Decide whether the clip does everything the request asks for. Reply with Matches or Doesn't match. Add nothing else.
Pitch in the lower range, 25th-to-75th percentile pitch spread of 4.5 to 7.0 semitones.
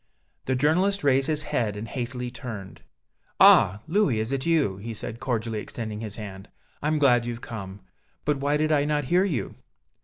Matches